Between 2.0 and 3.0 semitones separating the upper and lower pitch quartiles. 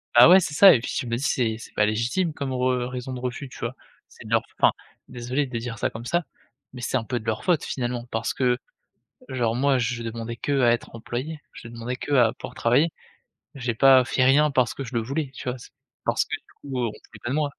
Yes: narrow, 2.6 semitones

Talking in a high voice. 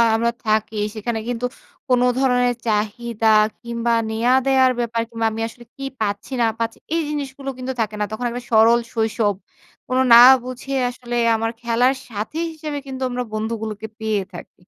Yes: high, 235 Hz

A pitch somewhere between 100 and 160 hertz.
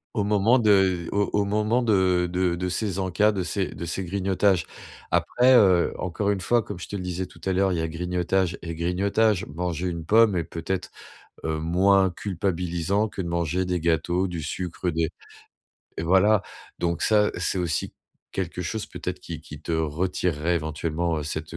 No: very low, 90 Hz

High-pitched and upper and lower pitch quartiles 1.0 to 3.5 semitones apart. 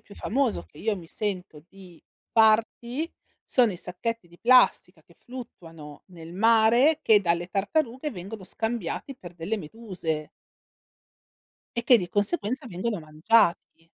No: high, 210 Hz; average, 5.2 semitones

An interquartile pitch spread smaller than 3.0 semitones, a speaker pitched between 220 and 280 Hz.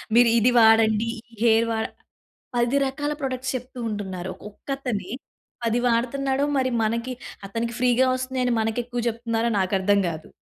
Yes: narrow, 2.6 semitones; high, 235 Hz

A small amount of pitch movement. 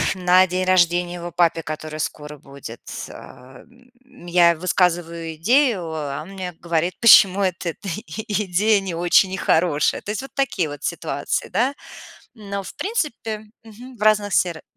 No: average, 3.9 semitones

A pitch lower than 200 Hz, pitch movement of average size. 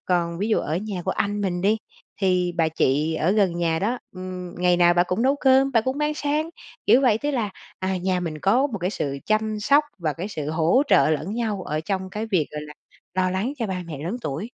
Yes: medium, 185 Hz; average, 4.5 semitones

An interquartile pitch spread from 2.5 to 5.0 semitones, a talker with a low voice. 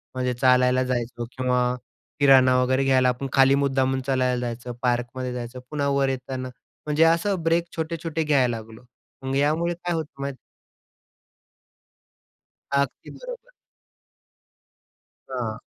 Yes: average, 2.8 semitones; low, 130 Hz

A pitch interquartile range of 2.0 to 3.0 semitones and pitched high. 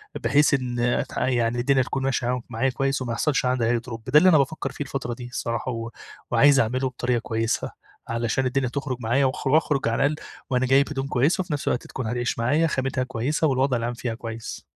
No: narrow, 2.4 semitones; low, 130 Hz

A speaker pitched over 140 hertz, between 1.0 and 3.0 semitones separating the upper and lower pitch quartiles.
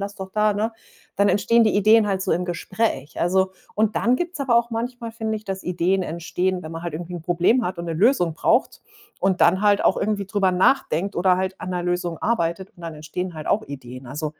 No: high, 190 Hz; average, 3.8 semitones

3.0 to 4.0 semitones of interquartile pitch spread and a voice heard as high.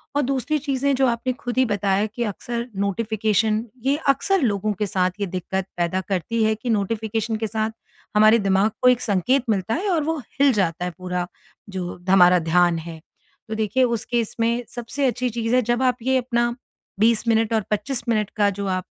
Yes: average, 3.7 semitones; high, 220 Hz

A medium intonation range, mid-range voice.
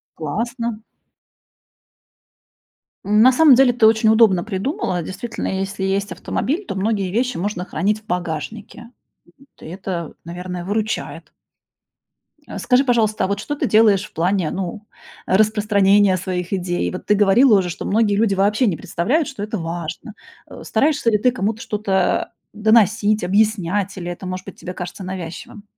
No: average, 3.2 semitones; high, 205 Hz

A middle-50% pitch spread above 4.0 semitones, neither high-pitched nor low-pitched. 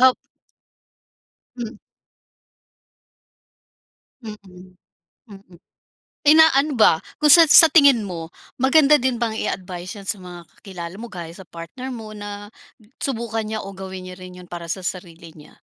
No: average, 5.3 semitones; high, 205 Hz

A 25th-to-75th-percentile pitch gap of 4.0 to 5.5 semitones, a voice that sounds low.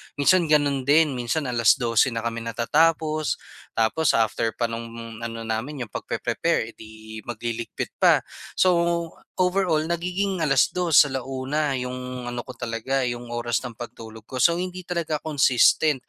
Yes: average, 4.9 semitones; low, 130 Hz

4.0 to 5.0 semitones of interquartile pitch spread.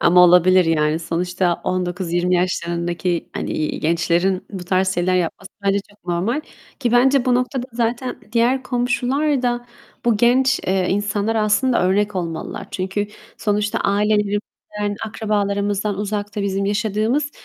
Yes: average, 4.3 semitones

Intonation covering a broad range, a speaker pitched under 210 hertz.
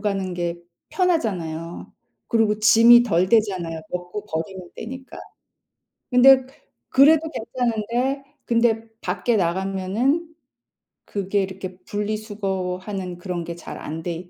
No: average, 4.5 semitones; high, 200 Hz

